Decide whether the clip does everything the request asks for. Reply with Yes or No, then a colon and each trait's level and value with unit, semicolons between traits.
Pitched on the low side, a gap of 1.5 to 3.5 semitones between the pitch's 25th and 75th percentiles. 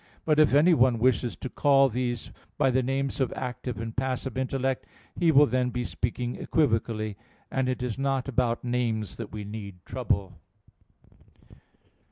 Yes: low, 125 Hz; average, 2.8 semitones